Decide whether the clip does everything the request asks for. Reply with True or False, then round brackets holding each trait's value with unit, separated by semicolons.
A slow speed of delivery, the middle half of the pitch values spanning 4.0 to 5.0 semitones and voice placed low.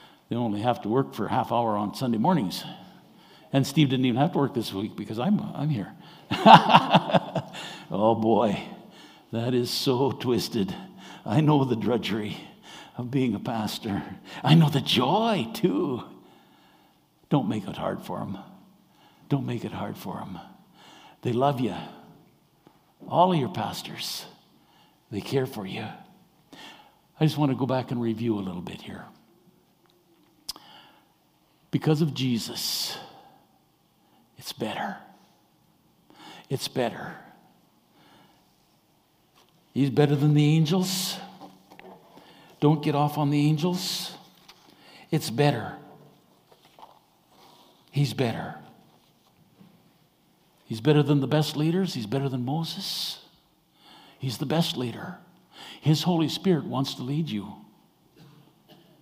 False (125 wpm; 4.7 semitones; 145 Hz)